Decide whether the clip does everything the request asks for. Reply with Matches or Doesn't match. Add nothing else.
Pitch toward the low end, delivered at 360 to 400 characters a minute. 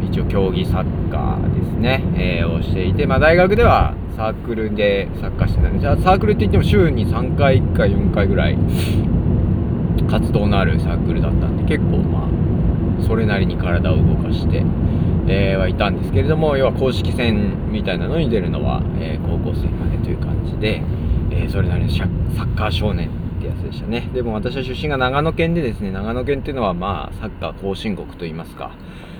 Matches